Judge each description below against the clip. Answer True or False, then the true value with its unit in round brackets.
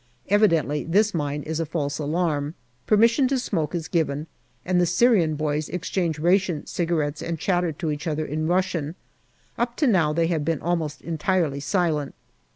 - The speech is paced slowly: False (165 wpm)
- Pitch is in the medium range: True (165 Hz)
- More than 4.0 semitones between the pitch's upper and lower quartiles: False (3.3 semitones)